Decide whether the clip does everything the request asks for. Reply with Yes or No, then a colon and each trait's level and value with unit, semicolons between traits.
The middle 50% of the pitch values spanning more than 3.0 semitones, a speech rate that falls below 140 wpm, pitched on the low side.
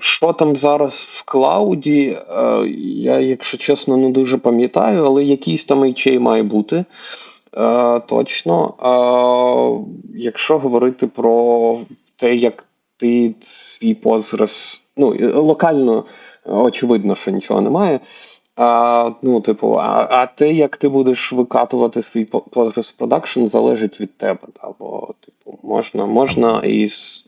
No: average, 2.7 semitones; average, 120 wpm; low, 125 Hz